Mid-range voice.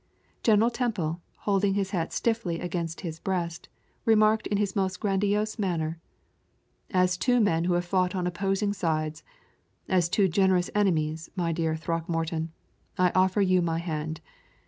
Yes: medium, 180 Hz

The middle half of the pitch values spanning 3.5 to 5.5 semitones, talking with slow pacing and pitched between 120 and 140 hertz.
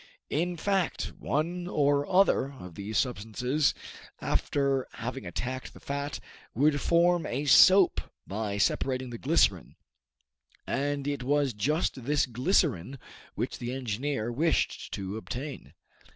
Yes: average, 3.9 semitones; slow, 125 wpm; low, 135 Hz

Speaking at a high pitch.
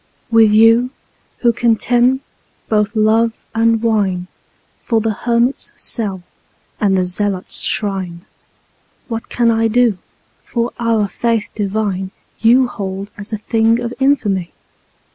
Yes: high, 225 Hz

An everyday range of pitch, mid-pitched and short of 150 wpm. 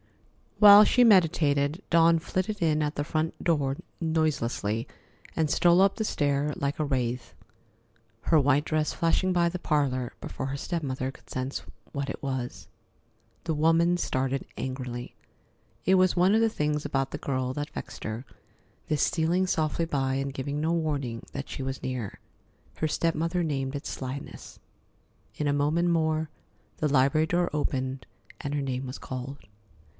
No: average, 3.7 semitones; medium, 150 Hz; average, 165 wpm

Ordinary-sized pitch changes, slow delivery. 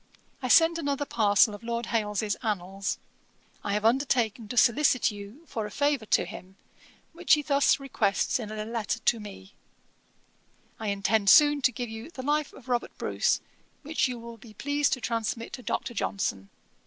No: average, 4.6 semitones; average, 175 wpm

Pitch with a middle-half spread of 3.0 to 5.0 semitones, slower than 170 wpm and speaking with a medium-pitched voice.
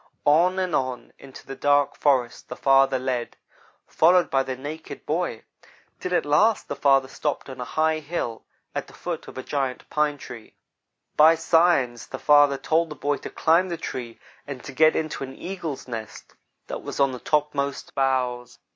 No: average, 3.3 semitones; average, 180 wpm; medium, 145 Hz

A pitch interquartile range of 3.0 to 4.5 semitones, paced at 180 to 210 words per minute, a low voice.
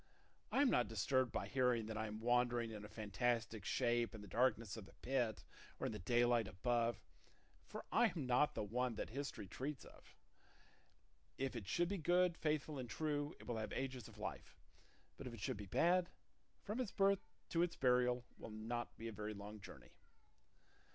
Yes: average, 4.0 semitones; average, 195 wpm; low, 120 Hz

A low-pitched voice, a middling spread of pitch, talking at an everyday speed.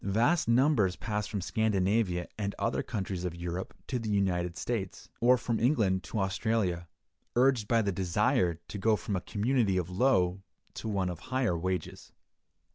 Yes: low, 100 Hz; average, 4.1 semitones; average, 165 wpm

